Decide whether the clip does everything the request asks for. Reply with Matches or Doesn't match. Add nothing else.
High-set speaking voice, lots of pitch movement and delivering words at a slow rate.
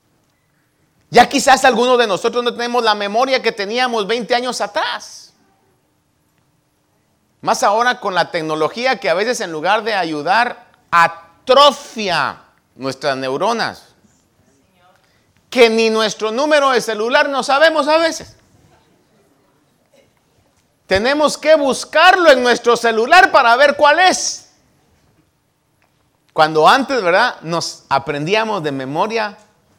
Matches